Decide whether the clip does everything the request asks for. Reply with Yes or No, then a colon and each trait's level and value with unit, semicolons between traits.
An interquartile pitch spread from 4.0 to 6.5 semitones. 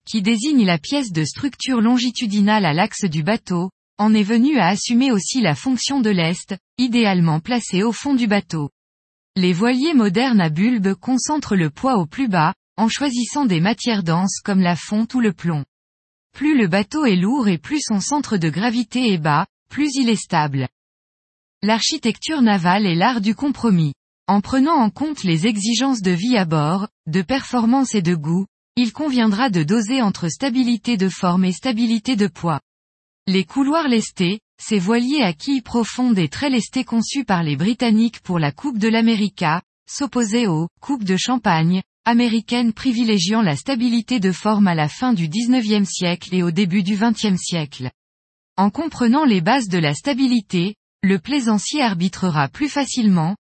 Yes: average, 5.3 semitones